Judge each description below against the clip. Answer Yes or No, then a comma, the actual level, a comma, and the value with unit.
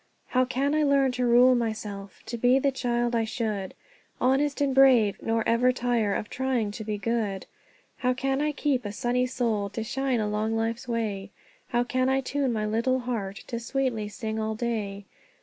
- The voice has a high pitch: Yes, high, 240 Hz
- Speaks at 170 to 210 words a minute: Yes, average, 185 wpm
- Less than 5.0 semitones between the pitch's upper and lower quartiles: Yes, average, 2.9 semitones